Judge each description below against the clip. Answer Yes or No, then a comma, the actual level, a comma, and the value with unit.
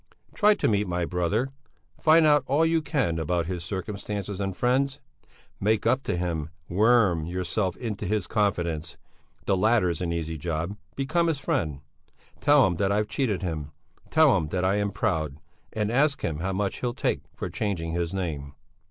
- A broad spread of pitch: Yes, wide, 6.0 semitones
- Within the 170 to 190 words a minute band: Yes, average, 175 wpm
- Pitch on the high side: No, very low, 95 Hz